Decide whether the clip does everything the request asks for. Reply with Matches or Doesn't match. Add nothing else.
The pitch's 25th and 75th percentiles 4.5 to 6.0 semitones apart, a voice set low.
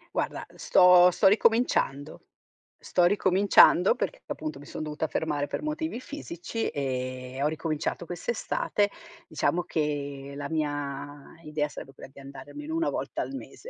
Doesn't match